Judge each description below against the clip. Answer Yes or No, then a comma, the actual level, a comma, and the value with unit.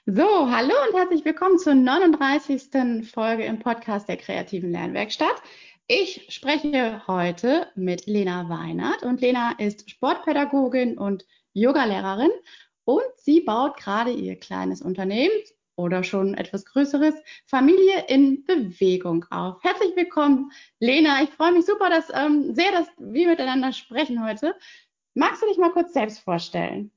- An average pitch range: No, wide, 8.1 semitones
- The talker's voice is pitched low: No, very high, 270 Hz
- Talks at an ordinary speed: Yes, average, 140 wpm